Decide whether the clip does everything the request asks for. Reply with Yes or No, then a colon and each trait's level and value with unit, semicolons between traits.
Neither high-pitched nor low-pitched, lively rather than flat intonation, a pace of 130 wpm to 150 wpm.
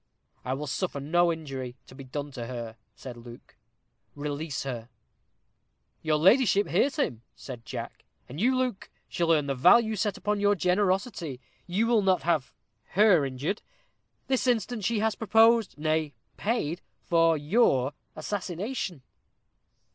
Yes: medium, 170 Hz; wide, 6.9 semitones; average, 140 wpm